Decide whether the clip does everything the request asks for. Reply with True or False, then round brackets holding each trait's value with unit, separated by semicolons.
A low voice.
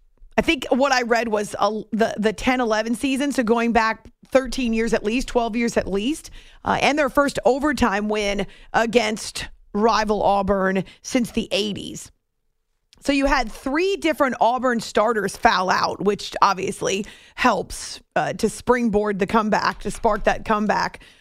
False (225 Hz)